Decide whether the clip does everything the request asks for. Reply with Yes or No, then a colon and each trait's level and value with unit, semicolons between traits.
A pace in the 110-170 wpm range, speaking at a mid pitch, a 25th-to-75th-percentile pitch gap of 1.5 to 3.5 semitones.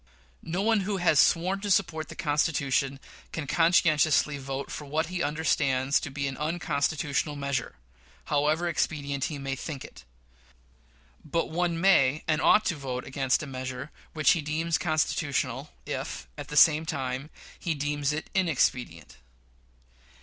Yes: average, 150 wpm; medium, 150 Hz; average, 3.0 semitones